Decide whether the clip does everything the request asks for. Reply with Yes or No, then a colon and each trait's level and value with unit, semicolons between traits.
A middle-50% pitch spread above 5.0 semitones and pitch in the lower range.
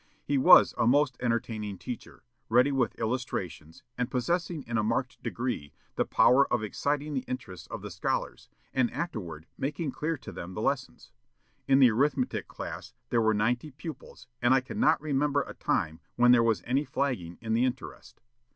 No: average, 3.8 semitones; low, 125 Hz